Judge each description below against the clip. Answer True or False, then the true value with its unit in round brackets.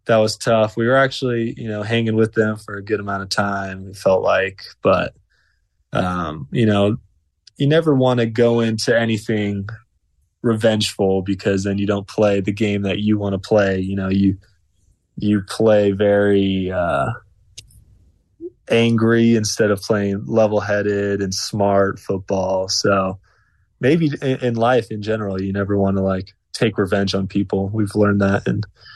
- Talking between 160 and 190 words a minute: True (165 wpm)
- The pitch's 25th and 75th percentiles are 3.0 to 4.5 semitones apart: False (2.4 semitones)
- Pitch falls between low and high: False (100 Hz)